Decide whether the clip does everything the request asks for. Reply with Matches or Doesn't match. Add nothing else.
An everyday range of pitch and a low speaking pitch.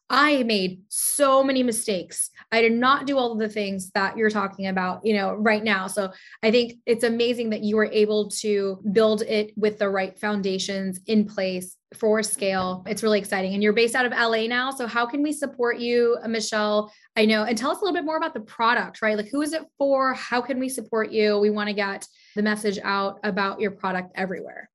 Doesn't match